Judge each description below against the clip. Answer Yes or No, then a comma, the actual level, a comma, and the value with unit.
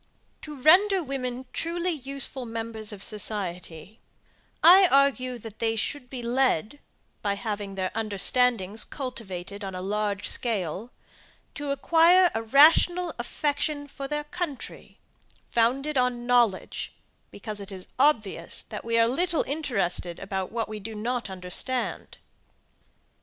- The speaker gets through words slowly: Yes, slow, 130 wpm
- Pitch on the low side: No, high, 240 Hz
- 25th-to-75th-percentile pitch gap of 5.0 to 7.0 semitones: Yes, wide, 5.5 semitones